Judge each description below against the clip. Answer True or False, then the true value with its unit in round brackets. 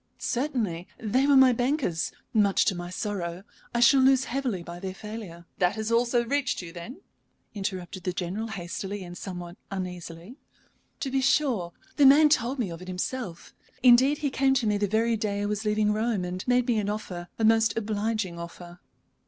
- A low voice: False (210 Hz)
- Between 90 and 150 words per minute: False (185 wpm)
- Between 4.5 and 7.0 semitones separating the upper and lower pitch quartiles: True (5.4 semitones)